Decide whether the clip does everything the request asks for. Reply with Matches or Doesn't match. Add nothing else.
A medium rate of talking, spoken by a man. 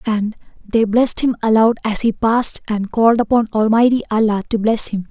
Doesn't match